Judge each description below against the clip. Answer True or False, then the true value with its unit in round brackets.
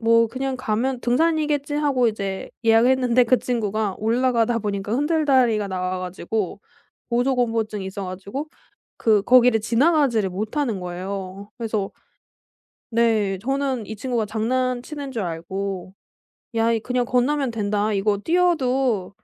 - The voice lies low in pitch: False (230 Hz)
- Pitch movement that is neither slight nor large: True (4.1 semitones)